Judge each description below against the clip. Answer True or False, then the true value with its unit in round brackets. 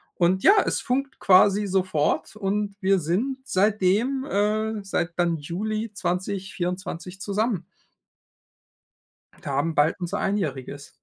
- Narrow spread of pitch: False (3.3 semitones)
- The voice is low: False (195 Hz)